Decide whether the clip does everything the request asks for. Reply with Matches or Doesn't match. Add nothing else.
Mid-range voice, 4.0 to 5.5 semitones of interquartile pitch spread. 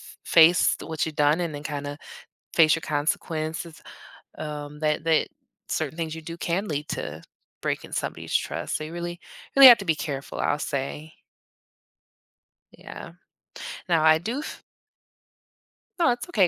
Doesn't match